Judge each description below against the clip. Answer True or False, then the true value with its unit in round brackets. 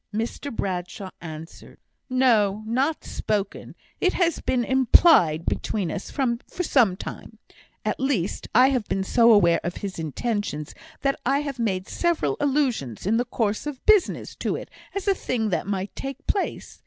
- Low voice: False (230 Hz)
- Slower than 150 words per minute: False (160 wpm)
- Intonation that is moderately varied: False (6.1 semitones)